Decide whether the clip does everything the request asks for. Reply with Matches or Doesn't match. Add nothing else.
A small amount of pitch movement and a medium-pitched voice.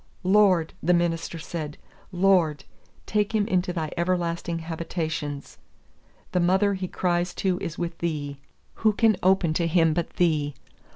Matches